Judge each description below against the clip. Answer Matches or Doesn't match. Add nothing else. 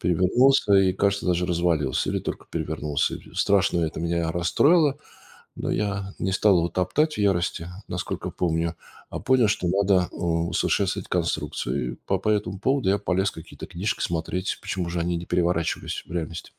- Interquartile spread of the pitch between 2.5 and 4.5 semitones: Matches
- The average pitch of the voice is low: Matches